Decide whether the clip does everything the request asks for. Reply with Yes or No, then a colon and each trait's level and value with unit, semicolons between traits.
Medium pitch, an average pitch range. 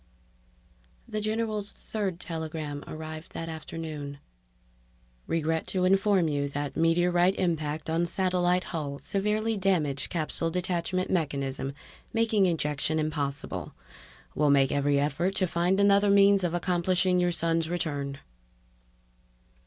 Yes: medium, 170 Hz; average, 3.7 semitones